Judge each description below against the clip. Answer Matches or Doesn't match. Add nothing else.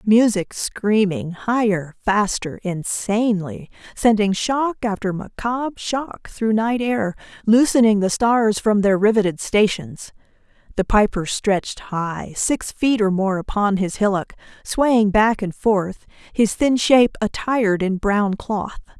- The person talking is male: Doesn't match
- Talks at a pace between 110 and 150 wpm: Matches